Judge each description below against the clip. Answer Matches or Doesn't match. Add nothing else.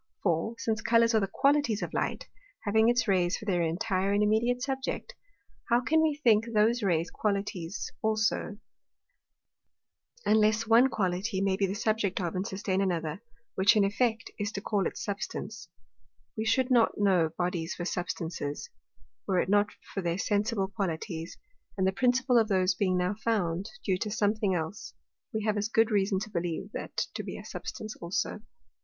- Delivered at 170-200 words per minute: Matches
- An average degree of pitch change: Matches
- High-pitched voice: Matches